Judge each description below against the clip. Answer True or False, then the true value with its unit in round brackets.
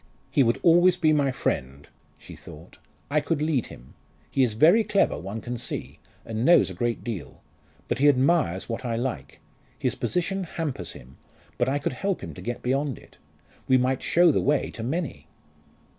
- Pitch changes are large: True (5.7 semitones)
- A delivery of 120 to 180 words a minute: False (190 wpm)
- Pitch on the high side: False (130 Hz)